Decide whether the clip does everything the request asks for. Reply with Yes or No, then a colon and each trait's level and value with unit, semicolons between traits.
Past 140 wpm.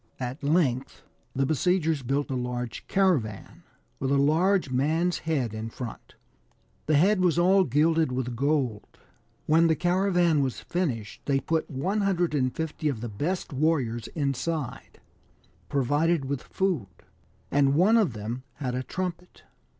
No: slow, 135 wpm